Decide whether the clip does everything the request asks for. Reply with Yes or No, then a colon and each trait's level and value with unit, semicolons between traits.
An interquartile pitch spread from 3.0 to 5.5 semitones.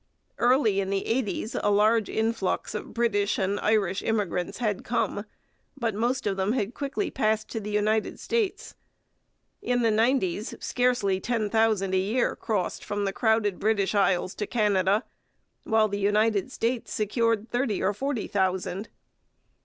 No: narrow, 2.5 semitones